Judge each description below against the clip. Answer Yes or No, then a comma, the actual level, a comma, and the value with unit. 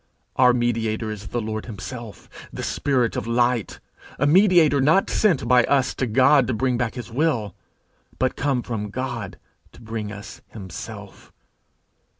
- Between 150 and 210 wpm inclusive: Yes, average, 155 wpm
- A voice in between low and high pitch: No, low, 120 Hz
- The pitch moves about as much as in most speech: Yes, average, 3.4 semitones